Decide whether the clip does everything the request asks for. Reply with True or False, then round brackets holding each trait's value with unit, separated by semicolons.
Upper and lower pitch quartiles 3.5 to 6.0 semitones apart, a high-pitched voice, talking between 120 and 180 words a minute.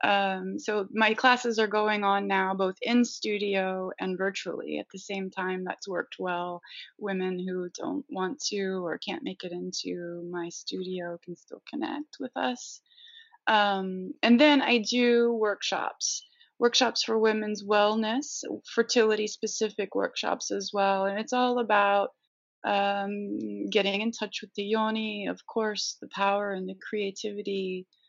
False (2.9 semitones; 205 Hz; 150 wpm)